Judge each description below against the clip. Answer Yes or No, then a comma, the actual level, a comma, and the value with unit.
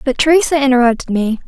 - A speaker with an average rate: Yes, average, 160 wpm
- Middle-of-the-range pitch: No, very high, 265 Hz